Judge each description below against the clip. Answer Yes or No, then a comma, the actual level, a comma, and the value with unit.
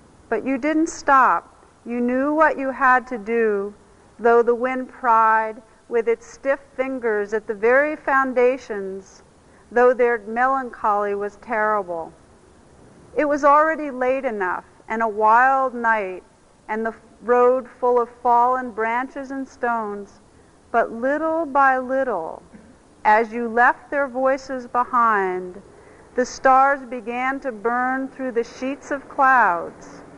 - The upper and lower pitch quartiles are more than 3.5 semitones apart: No, average, 2.9 semitones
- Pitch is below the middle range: No, very high, 250 Hz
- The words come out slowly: Yes, slow, 130 wpm